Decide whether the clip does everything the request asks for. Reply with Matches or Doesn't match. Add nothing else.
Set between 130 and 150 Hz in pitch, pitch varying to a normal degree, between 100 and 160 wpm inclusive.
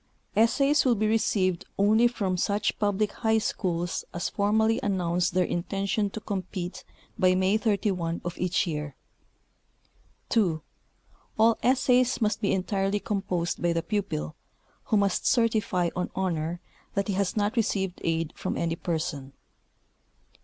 Doesn't match